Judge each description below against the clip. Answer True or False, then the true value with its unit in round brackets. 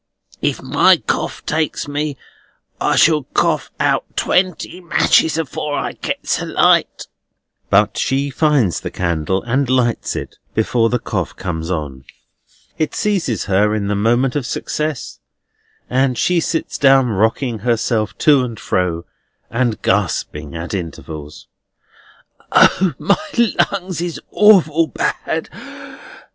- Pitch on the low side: True (125 Hz)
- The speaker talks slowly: True (130 wpm)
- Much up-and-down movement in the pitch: True (7.4 semitones)